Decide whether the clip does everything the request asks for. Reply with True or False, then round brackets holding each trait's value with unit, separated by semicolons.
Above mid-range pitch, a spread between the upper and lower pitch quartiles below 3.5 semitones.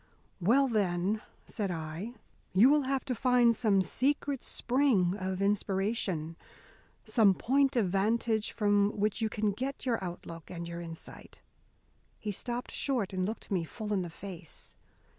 False (210 Hz; 4.4 semitones)